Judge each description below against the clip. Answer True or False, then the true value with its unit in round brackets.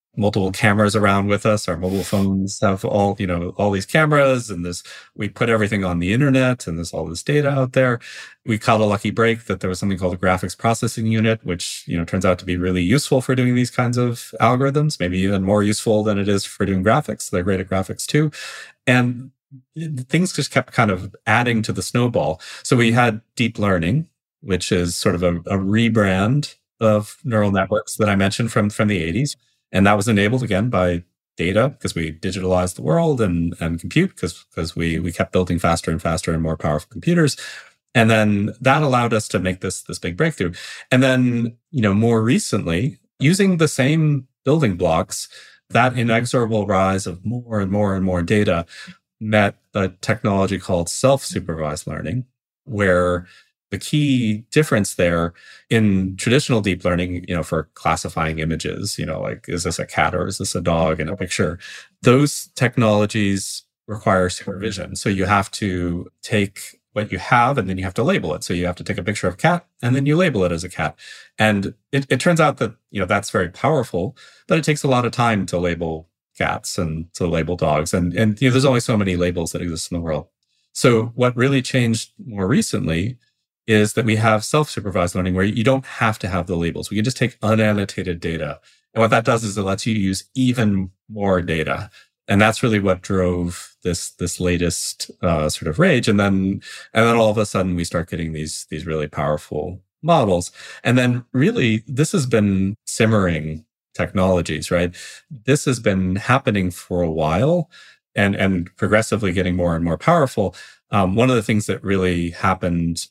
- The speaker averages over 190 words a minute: True (200 wpm)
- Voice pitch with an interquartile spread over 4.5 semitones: True (5.1 semitones)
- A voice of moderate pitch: False (105 Hz)